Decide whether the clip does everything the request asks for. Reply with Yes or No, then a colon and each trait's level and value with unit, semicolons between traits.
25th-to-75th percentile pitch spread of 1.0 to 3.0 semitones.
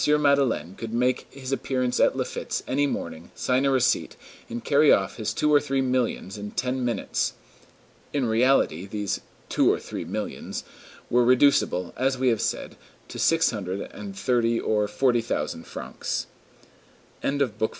No: average, 4.3 semitones